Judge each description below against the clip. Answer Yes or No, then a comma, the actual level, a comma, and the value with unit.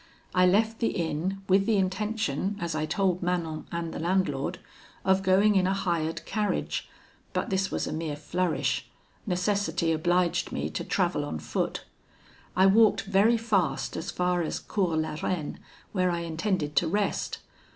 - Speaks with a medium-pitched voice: Yes, medium, 180 Hz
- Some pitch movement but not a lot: Yes, average, 3.2 semitones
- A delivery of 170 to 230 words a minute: No, average, 160 wpm